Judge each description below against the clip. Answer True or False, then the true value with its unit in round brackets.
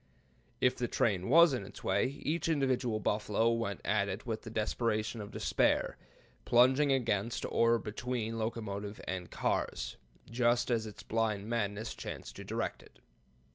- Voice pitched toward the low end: True (115 Hz)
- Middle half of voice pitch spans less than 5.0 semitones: True (2.8 semitones)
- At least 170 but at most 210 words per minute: False (150 wpm)